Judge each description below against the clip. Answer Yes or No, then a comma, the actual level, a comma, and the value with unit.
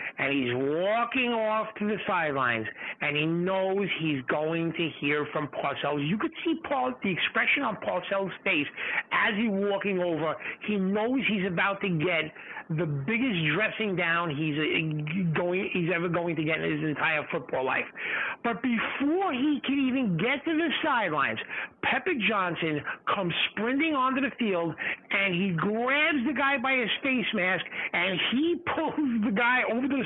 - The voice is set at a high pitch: Yes, high, 205 Hz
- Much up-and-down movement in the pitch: Yes, wide, 7.7 semitones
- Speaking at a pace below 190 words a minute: Yes, average, 170 wpm